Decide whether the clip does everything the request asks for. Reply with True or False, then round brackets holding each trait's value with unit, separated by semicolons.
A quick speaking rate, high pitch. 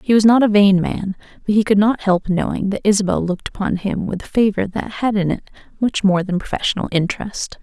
True (230 wpm; 200 Hz)